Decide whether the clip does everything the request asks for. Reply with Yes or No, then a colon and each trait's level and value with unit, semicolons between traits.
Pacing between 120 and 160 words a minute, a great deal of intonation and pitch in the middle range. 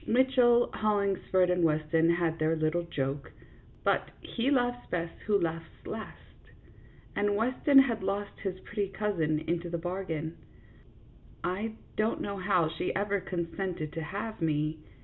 No: average, 145 wpm; average, 4.3 semitones; medium, 180 Hz